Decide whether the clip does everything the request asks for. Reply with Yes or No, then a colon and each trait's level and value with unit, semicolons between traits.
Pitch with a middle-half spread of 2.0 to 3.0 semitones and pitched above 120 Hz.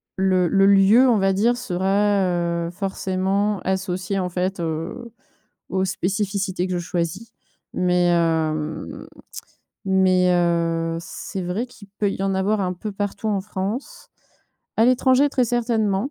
Yes: narrow, 2.6 semitones; high, 190 Hz